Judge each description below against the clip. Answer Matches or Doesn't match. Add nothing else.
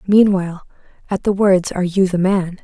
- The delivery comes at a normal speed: Matches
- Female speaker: Matches